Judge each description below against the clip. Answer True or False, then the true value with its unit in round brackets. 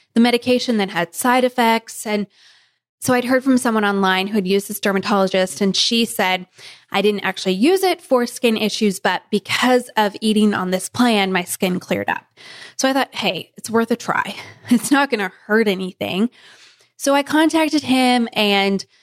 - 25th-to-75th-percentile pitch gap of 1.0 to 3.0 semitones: False (4.1 semitones)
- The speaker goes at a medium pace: True (185 wpm)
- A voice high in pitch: True (215 Hz)